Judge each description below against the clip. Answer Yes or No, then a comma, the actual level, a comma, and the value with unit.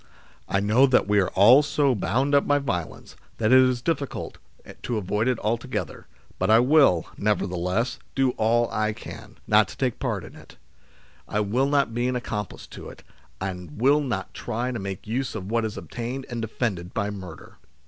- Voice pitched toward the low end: Yes, low, 115 Hz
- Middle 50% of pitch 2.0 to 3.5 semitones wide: No, average, 3.9 semitones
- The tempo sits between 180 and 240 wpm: Yes, average, 190 wpm